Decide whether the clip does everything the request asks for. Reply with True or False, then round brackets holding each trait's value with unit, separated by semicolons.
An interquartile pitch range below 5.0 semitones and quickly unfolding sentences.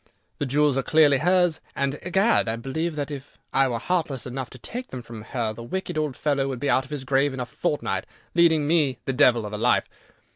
True (3.5 semitones; 230 wpm)